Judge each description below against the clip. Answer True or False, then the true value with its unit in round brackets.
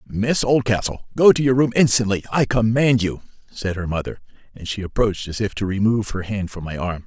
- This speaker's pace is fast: True (210 wpm)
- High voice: False (110 Hz)